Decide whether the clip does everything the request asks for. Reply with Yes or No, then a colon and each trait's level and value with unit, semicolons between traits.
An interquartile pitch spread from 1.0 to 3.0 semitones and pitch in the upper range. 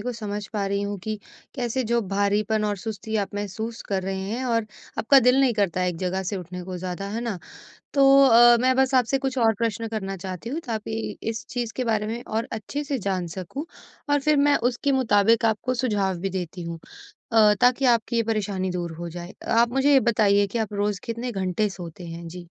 No: average, 3.7 semitones; high, 215 Hz